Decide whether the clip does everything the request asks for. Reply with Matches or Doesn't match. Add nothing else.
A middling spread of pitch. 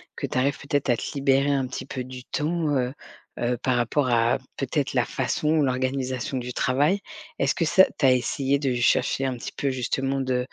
Doesn't match